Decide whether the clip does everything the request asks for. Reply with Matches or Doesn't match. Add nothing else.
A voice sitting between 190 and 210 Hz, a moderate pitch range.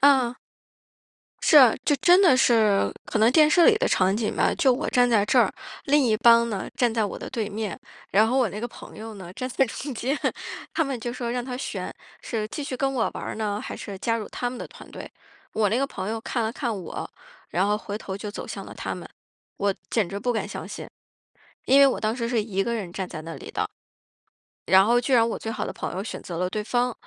Doesn't match